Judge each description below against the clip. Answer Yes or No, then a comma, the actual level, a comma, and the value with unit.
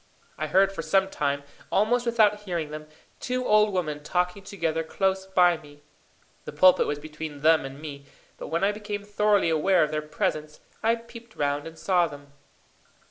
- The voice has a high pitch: No, medium, 175 Hz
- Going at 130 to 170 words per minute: No, average, 180 wpm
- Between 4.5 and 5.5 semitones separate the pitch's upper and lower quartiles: Yes, average, 5.1 semitones